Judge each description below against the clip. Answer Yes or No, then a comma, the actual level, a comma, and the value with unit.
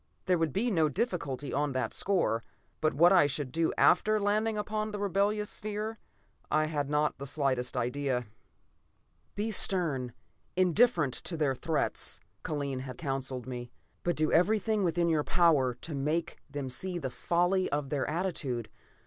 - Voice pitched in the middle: Yes, medium, 155 Hz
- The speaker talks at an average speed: Yes, average, 155 wpm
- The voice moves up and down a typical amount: No, wide, 5.7 semitones